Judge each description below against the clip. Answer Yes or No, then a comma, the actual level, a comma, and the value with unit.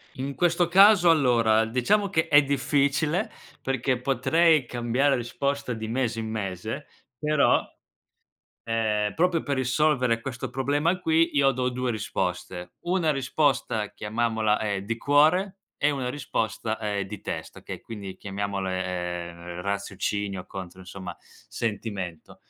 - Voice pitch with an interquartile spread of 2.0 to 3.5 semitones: No, wide, 5.9 semitones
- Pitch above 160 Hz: No, low, 120 Hz